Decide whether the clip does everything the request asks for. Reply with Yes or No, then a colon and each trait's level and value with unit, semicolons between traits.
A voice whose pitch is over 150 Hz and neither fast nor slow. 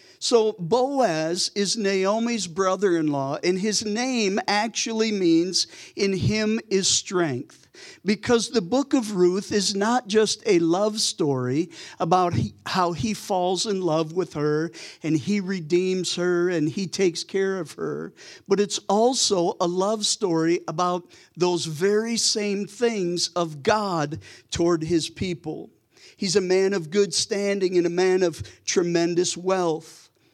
Yes: medium, 185 Hz; average, 145 wpm